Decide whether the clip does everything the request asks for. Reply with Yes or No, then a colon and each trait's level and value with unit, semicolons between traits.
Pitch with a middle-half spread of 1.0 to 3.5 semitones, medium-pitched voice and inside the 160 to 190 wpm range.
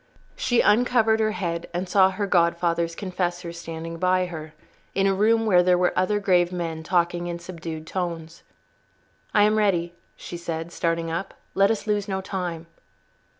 Yes: narrow, 2.6 semitones; medium, 180 Hz; average, 165 wpm